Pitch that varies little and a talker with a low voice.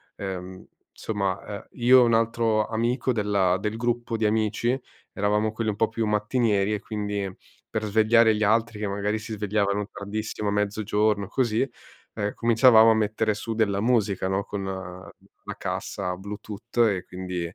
Yes: narrow, 1.9 semitones; low, 105 Hz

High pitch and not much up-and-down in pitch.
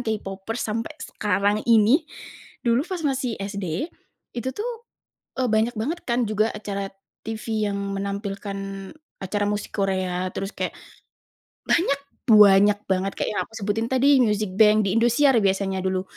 No: high, 210 Hz; average, 3.2 semitones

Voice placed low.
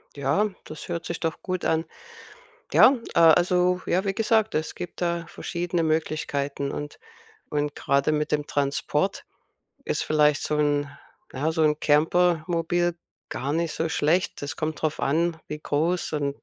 No: medium, 160 Hz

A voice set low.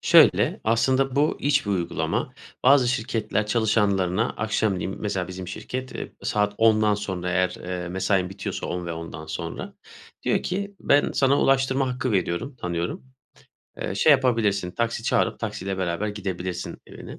Yes: low, 105 Hz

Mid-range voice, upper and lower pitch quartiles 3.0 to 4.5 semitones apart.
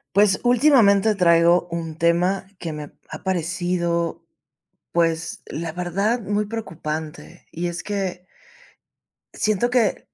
Yes: medium, 180 Hz; average, 3.3 semitones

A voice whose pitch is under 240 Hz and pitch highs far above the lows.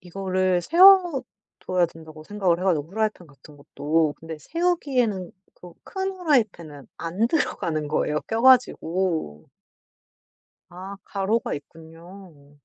Yes: medium, 185 Hz; wide, 5.9 semitones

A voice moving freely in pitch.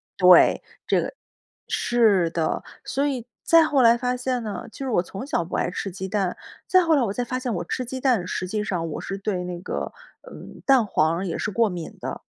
Yes: wide, 5.8 semitones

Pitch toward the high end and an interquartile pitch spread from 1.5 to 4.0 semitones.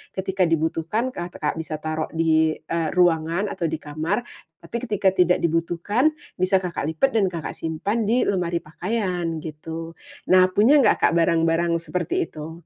No: medium, 170 Hz; average, 2.9 semitones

